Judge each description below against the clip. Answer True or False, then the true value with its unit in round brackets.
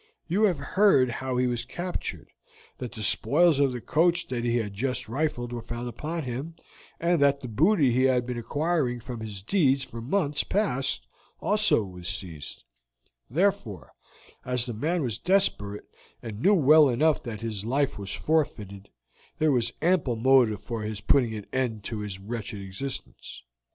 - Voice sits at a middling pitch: False (125 Hz)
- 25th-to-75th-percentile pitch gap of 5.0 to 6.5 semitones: True (5.6 semitones)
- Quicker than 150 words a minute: True (170 wpm)